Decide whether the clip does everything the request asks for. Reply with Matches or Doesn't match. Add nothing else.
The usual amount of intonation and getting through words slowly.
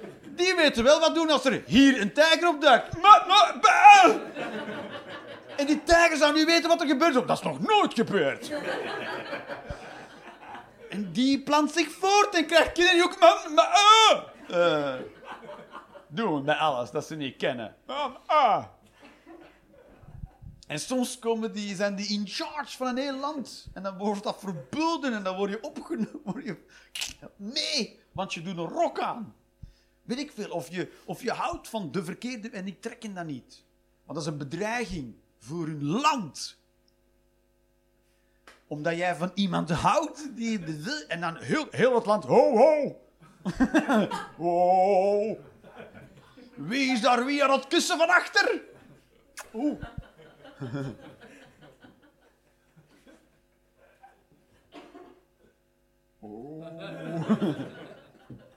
Doesn't match